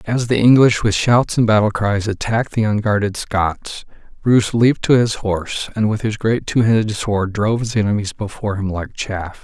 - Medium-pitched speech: No, low, 110 Hz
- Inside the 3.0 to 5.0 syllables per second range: No, 5.2 syllables/s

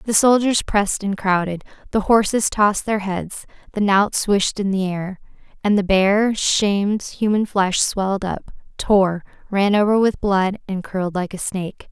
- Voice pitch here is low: No, high, 200 Hz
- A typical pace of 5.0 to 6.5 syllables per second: No, 4.5 syllables/s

